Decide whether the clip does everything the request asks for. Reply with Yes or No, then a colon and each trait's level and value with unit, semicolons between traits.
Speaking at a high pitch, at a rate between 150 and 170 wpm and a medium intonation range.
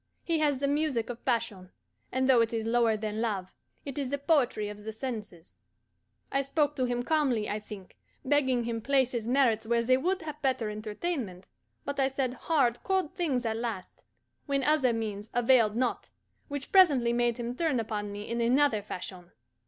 No: high, 245 Hz; average, 185 wpm; average, 4.1 semitones